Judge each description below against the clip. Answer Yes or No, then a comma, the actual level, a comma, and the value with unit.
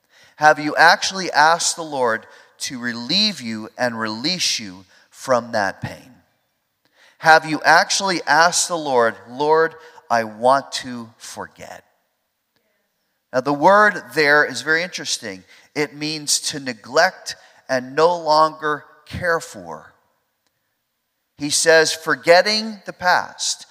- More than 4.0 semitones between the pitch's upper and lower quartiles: Yes, average, 4.6 semitones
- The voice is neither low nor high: Yes, medium, 150 Hz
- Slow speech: Yes, slow, 120 wpm